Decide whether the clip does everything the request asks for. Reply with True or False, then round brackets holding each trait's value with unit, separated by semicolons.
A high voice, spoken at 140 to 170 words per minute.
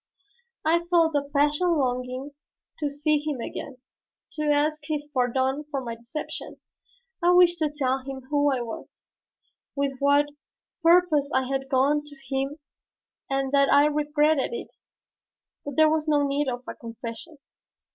True (290 Hz; 150 wpm)